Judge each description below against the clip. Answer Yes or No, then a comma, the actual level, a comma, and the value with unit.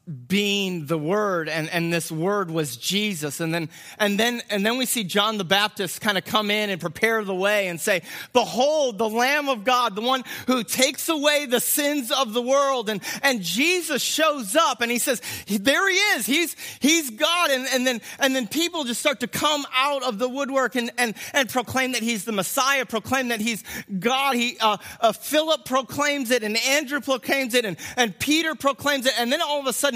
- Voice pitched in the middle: No, high, 245 Hz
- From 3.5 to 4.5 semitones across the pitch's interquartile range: No, average, 5.0 semitones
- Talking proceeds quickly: Yes, fast, 210 wpm